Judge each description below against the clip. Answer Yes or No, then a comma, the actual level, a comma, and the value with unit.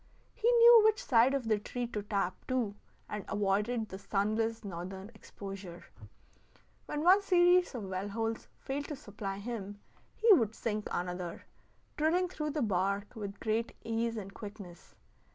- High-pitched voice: Yes, high, 220 Hz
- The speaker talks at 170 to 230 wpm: No, average, 150 wpm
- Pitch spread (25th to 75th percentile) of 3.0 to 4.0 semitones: No, average, 5.2 semitones